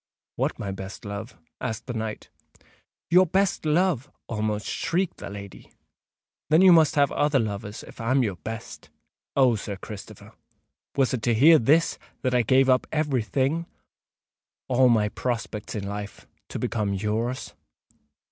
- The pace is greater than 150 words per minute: No, average, 145 wpm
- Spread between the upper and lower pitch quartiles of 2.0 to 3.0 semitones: No, wide, 5.6 semitones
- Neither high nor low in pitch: No, low, 120 Hz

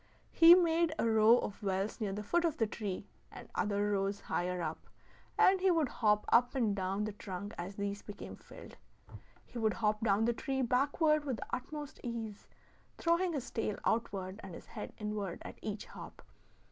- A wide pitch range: No, average, 4.8 semitones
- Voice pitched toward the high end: Yes, high, 215 Hz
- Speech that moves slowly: No, average, 185 wpm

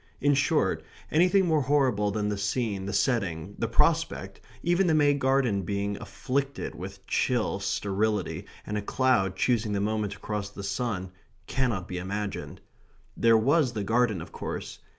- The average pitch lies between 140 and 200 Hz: No, low, 110 Hz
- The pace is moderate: Yes, average, 160 wpm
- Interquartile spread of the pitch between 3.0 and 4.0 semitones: No, average, 4.9 semitones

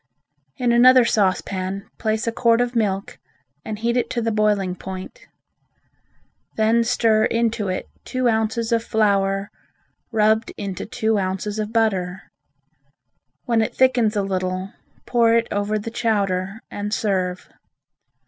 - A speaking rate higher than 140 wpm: No, slow, 135 wpm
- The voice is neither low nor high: No, high, 215 Hz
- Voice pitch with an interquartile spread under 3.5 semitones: Yes, average, 2.8 semitones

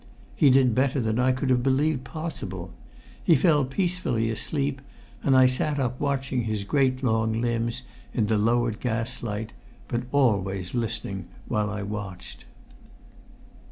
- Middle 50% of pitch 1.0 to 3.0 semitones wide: No, average, 3.6 semitones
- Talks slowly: No, average, 145 wpm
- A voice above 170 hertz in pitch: No, low, 120 Hz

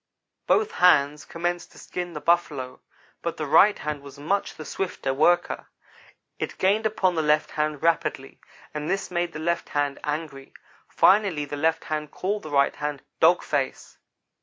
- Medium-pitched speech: Yes, medium, 155 Hz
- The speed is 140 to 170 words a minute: Yes, average, 165 wpm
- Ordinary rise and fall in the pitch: Yes, average, 3.1 semitones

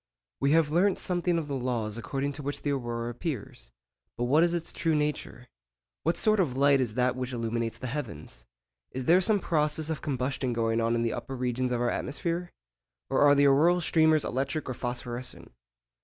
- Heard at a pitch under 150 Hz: Yes, low, 135 Hz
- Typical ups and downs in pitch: Yes, average, 4.5 semitones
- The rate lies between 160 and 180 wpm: No, average, 195 wpm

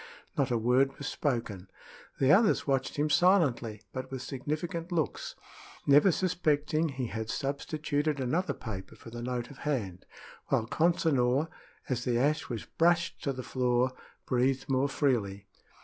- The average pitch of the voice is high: No, low, 135 Hz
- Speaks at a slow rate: No, average, 150 wpm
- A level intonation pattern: No, average, 3.9 semitones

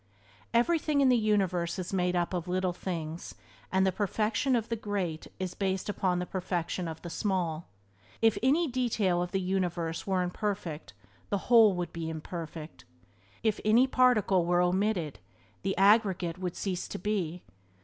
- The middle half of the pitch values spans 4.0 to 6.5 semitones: No, average, 3.4 semitones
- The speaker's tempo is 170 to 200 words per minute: No, average, 160 wpm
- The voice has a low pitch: No, medium, 185 Hz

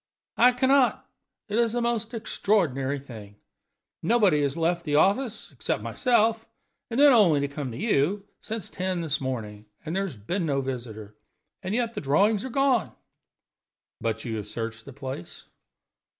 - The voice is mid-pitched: Yes, medium, 170 Hz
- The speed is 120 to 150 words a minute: No, average, 165 wpm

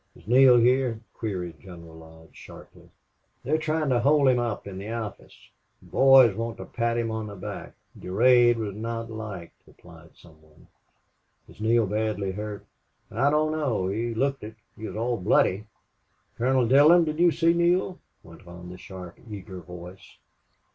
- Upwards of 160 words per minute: Yes, average, 170 wpm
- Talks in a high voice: No, low, 110 Hz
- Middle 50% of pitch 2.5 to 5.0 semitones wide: No, wide, 5.4 semitones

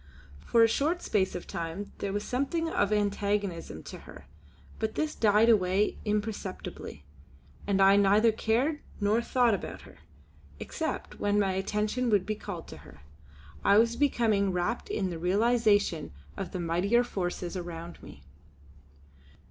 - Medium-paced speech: Yes, average, 150 wpm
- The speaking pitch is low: No, high, 205 Hz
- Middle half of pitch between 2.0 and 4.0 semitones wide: Yes, average, 3.4 semitones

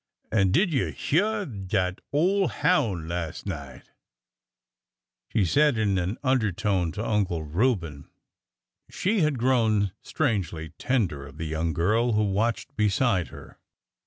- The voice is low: Yes, low, 105 Hz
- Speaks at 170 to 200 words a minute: No, slow, 135 wpm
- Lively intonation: Yes, wide, 7.2 semitones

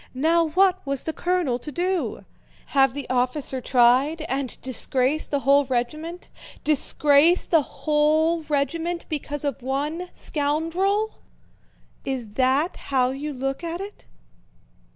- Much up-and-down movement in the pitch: No, average, 3.8 semitones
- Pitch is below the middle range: No, very high, 295 Hz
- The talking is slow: Yes, slow, 125 wpm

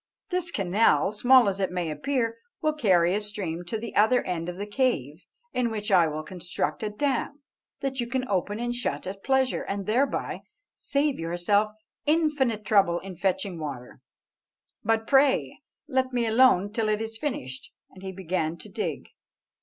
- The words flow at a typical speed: Yes, average, 170 wpm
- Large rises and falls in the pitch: Yes, wide, 5.8 semitones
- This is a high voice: Yes, high, 210 Hz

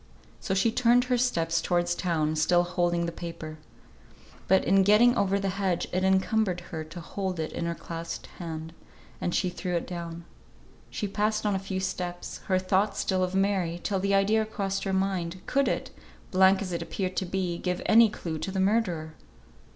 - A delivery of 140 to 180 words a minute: No, average, 190 wpm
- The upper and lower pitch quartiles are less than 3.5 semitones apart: Yes, narrow, 2.4 semitones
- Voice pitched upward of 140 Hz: Yes, medium, 185 Hz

